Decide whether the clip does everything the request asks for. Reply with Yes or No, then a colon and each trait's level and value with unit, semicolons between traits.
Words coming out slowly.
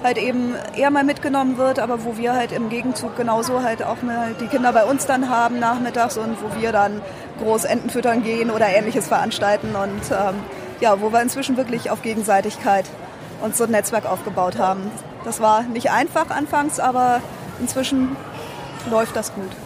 No: average, 175 wpm